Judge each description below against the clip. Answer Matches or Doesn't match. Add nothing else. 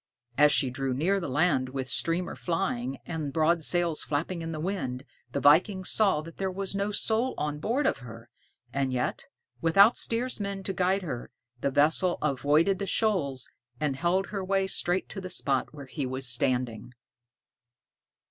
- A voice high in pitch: Doesn't match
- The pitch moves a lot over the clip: Matches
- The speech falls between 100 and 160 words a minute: Doesn't match